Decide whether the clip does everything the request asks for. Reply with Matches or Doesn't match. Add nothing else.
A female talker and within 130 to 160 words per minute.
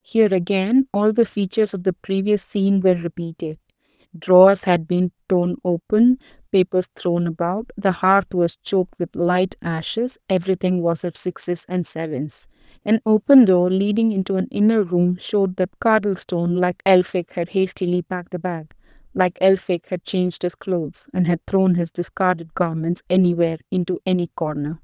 Matches